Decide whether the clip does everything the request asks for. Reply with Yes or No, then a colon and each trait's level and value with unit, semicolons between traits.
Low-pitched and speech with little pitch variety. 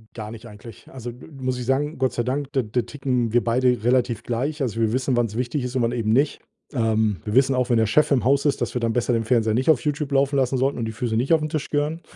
No: low, 125 Hz; average, 3.0 semitones